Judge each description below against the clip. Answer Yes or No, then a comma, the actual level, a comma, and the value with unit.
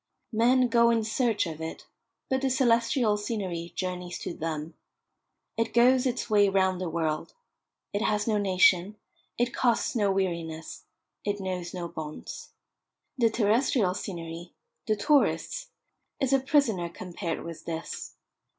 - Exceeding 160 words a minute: No, average, 140 wpm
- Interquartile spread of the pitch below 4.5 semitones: No, wide, 5.4 semitones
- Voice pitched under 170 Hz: No, high, 205 Hz